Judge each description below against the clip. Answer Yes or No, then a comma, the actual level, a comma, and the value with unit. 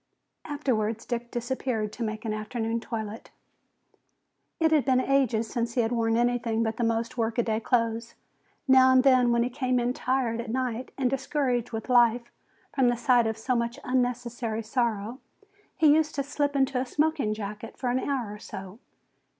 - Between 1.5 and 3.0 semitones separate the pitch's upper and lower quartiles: Yes, narrow, 2.4 semitones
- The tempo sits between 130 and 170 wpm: No, average, 180 wpm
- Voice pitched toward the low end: No, high, 240 Hz